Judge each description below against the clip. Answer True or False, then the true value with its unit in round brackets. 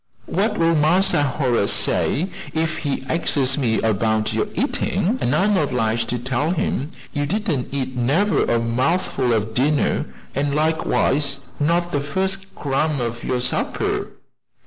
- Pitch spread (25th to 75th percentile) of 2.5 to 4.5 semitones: False (4.9 semitones)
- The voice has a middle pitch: True (145 Hz)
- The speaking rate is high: False (145 wpm)